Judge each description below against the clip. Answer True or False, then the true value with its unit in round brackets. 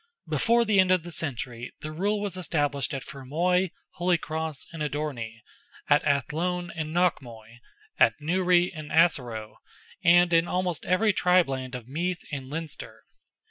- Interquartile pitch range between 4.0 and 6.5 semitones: True (4.5 semitones)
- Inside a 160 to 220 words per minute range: False (145 wpm)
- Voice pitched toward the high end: False (160 Hz)